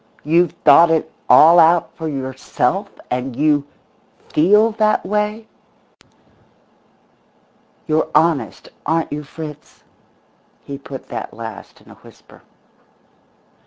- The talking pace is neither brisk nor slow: No, slow, 105 wpm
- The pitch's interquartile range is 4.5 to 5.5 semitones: No, average, 3.7 semitones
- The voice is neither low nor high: Yes, medium, 155 Hz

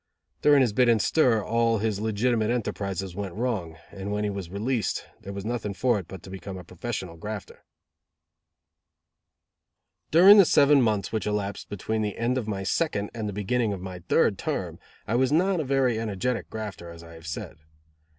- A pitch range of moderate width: Yes, average, 3.9 semitones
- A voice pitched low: Yes, low, 105 Hz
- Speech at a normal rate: Yes, average, 190 wpm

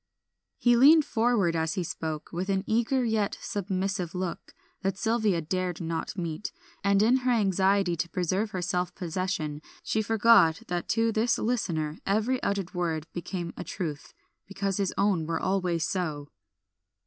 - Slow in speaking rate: No, average, 155 wpm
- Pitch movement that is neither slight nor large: Yes, average, 4.1 semitones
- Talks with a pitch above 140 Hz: Yes, high, 190 Hz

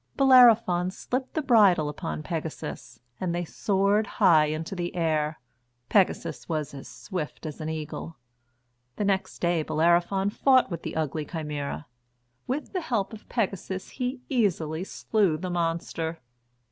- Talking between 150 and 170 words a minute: No, average, 140 wpm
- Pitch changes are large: No, average, 4.8 semitones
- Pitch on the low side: No, medium, 175 Hz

